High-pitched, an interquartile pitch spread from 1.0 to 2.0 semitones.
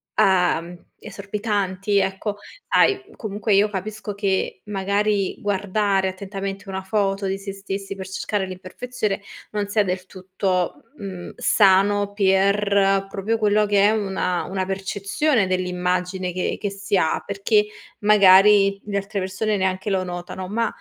Yes: high, 195 Hz; narrow, 1.4 semitones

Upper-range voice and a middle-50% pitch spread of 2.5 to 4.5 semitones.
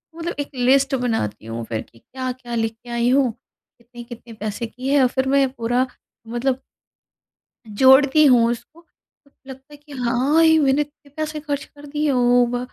Yes: very high, 255 Hz; average, 2.9 semitones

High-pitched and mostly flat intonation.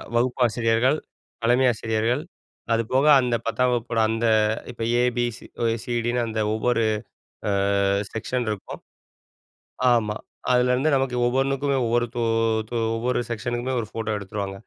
No: low, 120 Hz; narrow, 1.9 semitones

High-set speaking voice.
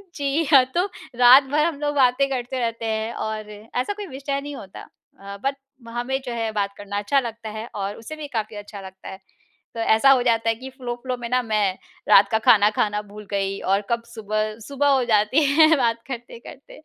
Yes: high, 235 Hz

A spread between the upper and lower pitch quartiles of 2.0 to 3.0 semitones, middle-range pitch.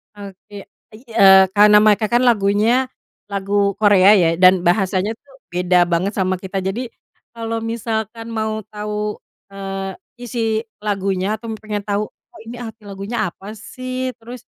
No: average, 2.7 semitones; high, 210 Hz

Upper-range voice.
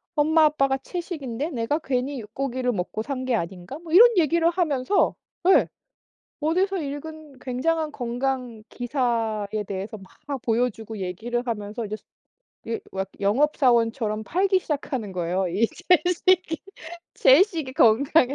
Yes: very high, 260 Hz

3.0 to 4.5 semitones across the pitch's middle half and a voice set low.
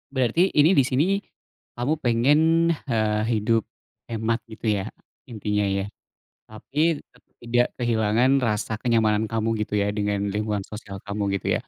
Yes: average, 3.5 semitones; low, 115 Hz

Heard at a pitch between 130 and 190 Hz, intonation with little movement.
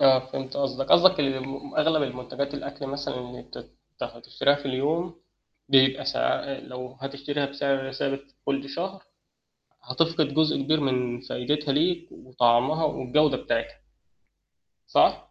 Yes: medium, 140 Hz; narrow, 2.3 semitones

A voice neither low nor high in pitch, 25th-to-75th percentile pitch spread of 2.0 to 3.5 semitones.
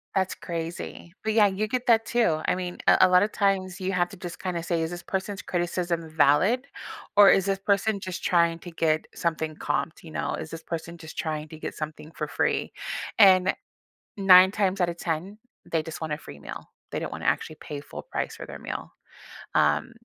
Yes: medium, 175 Hz; average, 3.1 semitones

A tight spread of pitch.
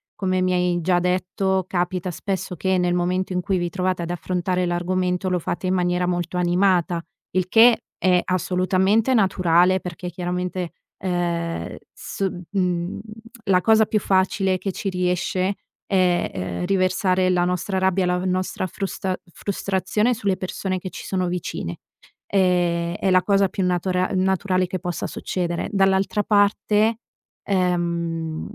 Yes: narrow, 1.3 semitones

